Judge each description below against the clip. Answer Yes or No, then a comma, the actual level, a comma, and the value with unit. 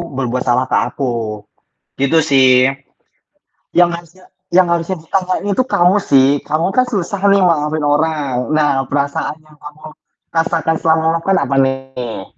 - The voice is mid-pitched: Yes, medium, 155 Hz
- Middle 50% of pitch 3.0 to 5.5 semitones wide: Yes, average, 4.4 semitones